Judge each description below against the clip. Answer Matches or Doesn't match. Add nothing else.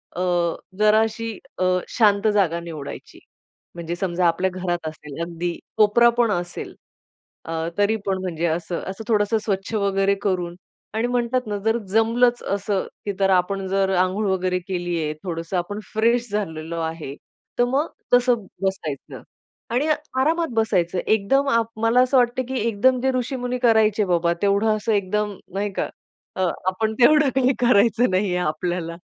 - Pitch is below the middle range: Doesn't match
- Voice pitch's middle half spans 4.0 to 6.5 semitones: Matches